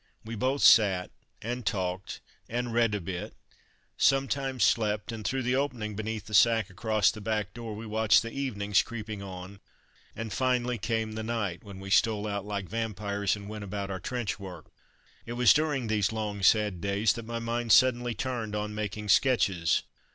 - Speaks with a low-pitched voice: Yes, low, 110 Hz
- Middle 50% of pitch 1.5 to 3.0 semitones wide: Yes, average, 2.7 semitones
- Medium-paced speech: Yes, average, 180 wpm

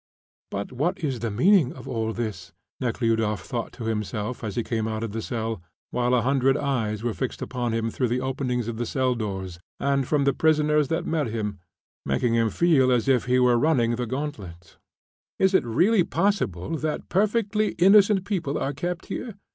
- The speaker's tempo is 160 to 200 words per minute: Yes, average, 190 wpm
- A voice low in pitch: Yes, low, 125 Hz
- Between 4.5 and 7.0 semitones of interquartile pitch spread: Yes, average, 5.1 semitones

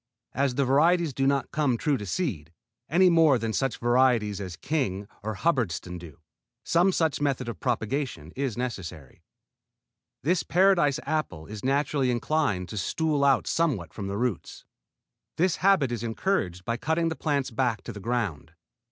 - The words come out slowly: No, average, 160 wpm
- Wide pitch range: Yes, wide, 6.6 semitones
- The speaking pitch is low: Yes, low, 130 Hz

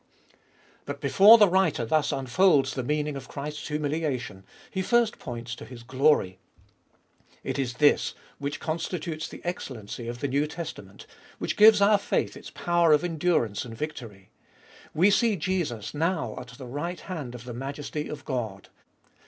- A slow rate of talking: No, average, 160 wpm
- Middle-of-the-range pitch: Yes, medium, 145 Hz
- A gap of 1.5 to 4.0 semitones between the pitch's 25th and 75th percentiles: No, wide, 5.6 semitones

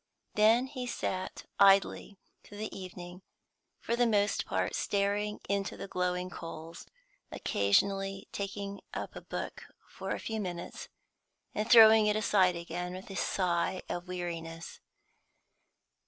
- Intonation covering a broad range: No, average, 2.8 semitones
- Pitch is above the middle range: Yes, high, 195 Hz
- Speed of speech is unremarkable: No, slow, 130 wpm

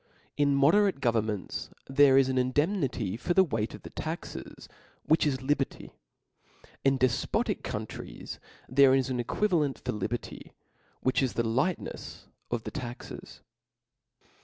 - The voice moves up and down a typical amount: Yes, average, 3.3 semitones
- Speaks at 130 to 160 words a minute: Yes, average, 140 wpm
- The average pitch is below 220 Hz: Yes, low, 135 Hz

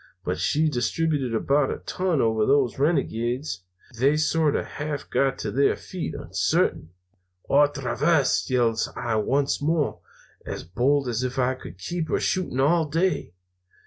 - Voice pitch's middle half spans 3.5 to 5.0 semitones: Yes, average, 4.1 semitones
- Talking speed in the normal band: Yes, average, 150 wpm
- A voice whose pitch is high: No, medium, 140 Hz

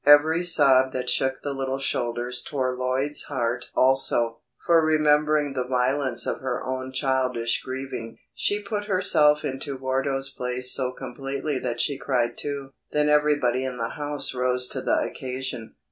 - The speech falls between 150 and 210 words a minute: Yes, average, 155 wpm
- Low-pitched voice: Yes, low, 130 Hz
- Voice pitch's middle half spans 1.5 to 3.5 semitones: Yes, narrow, 2.5 semitones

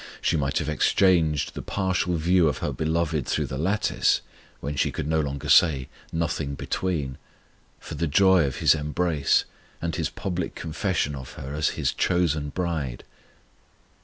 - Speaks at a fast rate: No, average, 160 wpm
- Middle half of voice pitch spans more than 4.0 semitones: No, average, 3.4 semitones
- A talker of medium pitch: No, very low, 80 Hz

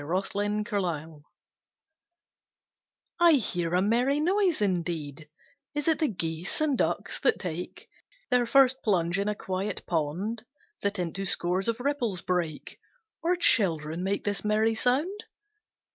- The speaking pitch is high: Yes, high, 200 Hz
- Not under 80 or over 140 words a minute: Yes, slow, 135 wpm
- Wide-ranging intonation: Yes, wide, 6.2 semitones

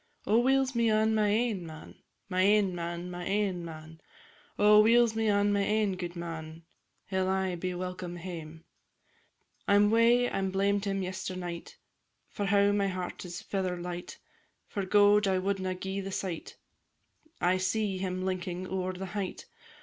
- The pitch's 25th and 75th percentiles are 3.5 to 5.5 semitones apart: No, narrow, 2.4 semitones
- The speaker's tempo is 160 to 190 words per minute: Yes, average, 165 wpm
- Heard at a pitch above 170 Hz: Yes, high, 190 Hz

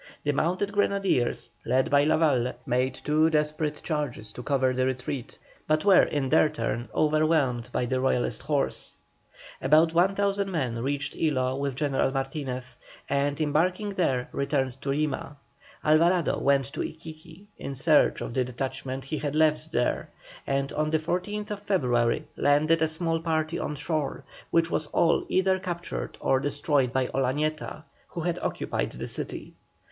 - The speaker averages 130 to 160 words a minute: Yes, average, 150 wpm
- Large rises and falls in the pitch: No, average, 3.5 semitones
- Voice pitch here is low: No, medium, 150 Hz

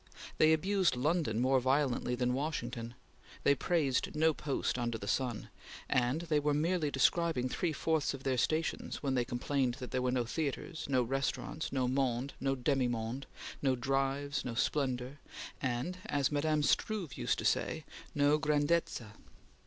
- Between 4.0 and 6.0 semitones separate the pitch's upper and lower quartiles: No, average, 3.4 semitones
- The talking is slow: No, average, 160 wpm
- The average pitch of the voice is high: No, low, 135 Hz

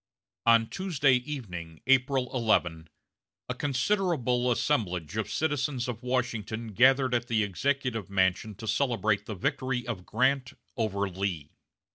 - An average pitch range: Yes, average, 4.6 semitones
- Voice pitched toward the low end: Yes, low, 120 Hz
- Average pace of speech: No, slow, 125 wpm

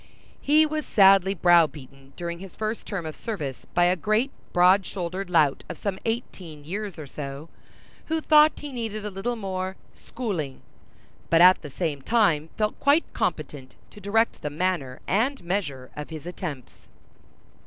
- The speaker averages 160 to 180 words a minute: Yes, average, 165 wpm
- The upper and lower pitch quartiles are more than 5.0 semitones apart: Yes, wide, 5.6 semitones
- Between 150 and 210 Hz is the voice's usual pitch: Yes, medium, 185 Hz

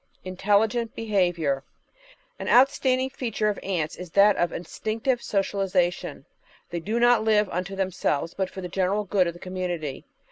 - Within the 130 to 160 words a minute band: Yes, average, 155 wpm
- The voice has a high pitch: Yes, high, 195 Hz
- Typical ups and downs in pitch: Yes, average, 3.6 semitones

